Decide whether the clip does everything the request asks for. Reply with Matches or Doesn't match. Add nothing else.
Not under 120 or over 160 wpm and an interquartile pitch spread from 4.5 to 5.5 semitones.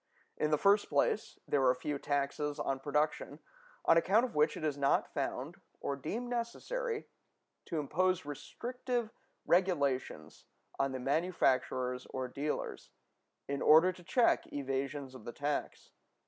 Matches